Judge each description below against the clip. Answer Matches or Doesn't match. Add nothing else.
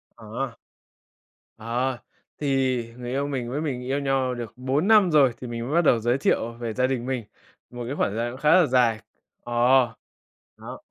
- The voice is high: Doesn't match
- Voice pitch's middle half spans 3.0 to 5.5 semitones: Doesn't match